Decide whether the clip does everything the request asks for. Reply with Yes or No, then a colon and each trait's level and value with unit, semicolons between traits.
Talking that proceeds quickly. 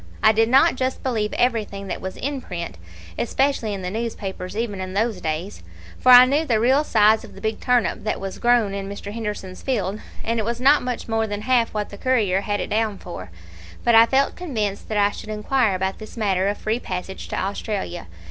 Yes: fast, 215 wpm